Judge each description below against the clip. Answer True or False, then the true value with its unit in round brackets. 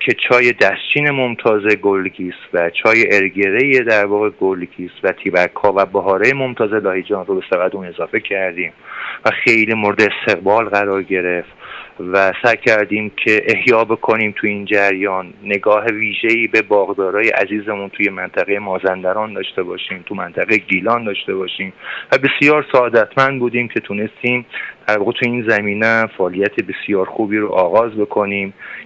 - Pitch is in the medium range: False (105 Hz)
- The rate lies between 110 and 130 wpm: False (145 wpm)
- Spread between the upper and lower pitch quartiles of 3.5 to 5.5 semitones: False (2.8 semitones)